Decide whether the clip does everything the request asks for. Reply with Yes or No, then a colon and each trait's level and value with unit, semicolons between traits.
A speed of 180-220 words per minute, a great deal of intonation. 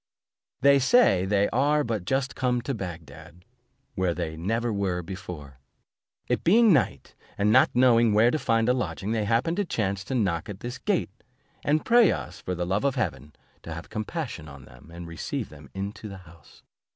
Yes: average, 190 wpm; wide, 6.8 semitones